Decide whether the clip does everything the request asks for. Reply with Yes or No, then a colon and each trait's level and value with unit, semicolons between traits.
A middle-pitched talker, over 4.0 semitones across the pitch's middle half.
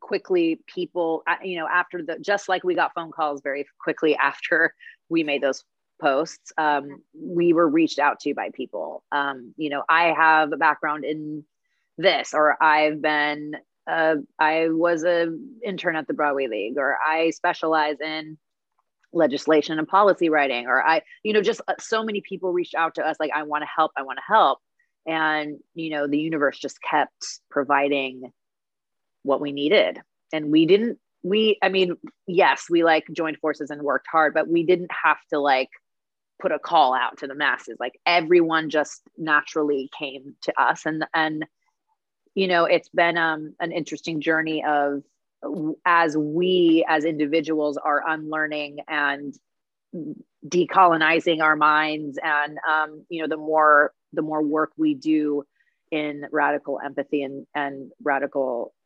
No: medium, 155 Hz; narrow, 2.4 semitones